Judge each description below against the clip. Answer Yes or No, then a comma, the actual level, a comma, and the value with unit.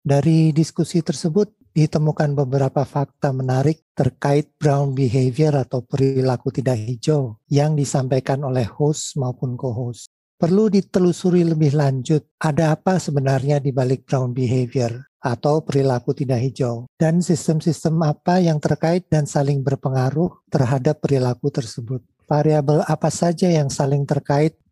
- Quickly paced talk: No, average, 125 wpm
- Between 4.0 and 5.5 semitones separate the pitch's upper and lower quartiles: No, average, 3.1 semitones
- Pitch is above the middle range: No, medium, 145 Hz